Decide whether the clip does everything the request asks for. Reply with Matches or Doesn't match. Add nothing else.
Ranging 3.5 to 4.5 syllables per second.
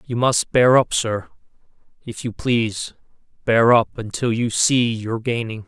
Matches